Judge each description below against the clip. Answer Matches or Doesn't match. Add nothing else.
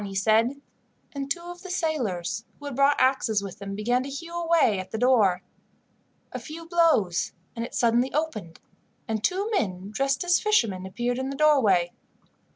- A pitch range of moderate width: Doesn't match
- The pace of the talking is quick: Doesn't match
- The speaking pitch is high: Matches